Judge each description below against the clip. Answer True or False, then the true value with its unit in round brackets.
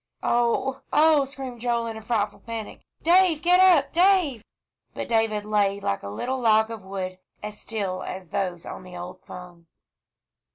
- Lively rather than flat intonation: True (5.8 semitones)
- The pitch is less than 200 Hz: False (220 Hz)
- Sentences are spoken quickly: False (165 wpm)